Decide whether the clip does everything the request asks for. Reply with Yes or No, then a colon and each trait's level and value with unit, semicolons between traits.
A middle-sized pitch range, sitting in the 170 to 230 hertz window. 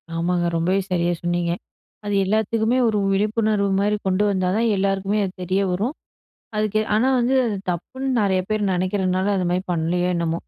Yes: average, 3.1 semitones; high, 195 Hz